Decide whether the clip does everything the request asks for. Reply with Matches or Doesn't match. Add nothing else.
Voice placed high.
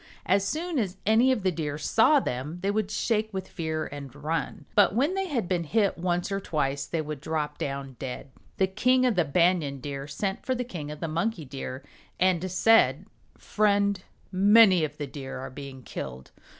Doesn't match